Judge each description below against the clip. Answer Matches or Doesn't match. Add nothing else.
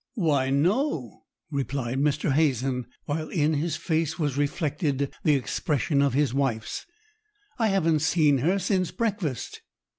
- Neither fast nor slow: Doesn't match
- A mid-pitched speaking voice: Matches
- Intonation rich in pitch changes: Doesn't match